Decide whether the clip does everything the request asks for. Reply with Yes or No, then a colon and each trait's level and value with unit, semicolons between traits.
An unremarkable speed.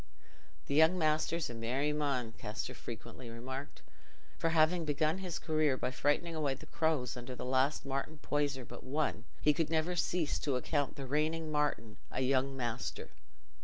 Yes: average, 165 wpm